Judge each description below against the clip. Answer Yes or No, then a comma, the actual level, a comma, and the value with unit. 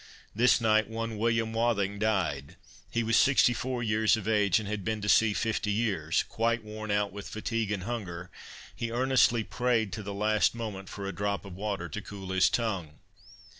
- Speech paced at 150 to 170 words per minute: No, average, 185 wpm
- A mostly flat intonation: Yes, narrow, 2.3 semitones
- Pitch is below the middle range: Yes, low, 110 Hz